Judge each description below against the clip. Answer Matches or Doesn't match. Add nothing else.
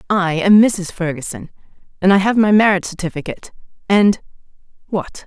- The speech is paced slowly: Matches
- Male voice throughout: Doesn't match